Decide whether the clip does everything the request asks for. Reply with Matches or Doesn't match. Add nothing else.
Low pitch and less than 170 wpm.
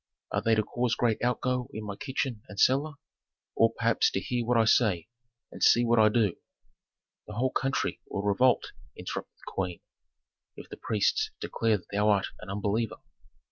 Doesn't match